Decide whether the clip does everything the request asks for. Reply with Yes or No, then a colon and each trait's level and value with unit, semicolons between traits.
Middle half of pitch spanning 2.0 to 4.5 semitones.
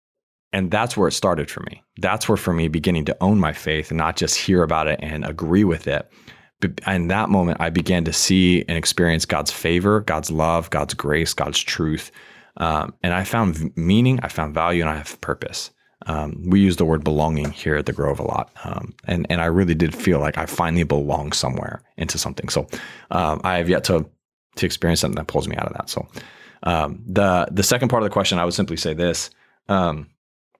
Yes: average, 2.9 semitones